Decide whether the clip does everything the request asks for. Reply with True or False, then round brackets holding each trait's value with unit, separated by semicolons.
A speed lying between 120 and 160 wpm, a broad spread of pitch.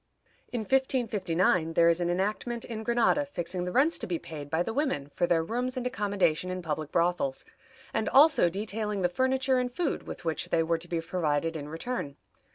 False (195 wpm; 6.8 semitones)